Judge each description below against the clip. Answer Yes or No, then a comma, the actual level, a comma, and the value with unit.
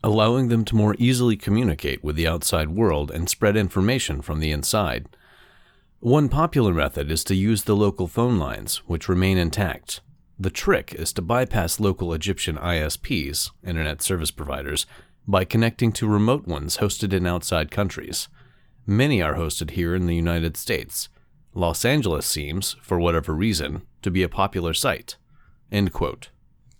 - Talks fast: No, average, 155 wpm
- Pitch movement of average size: Yes, average, 5.0 semitones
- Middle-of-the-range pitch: No, very low, 95 Hz